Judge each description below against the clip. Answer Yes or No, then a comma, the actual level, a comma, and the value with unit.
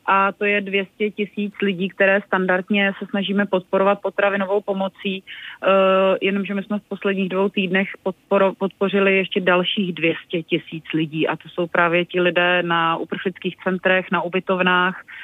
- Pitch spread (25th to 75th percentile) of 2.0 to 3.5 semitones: No, narrow, 1.6 semitones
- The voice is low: No, high, 190 Hz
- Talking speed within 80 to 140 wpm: No, average, 150 wpm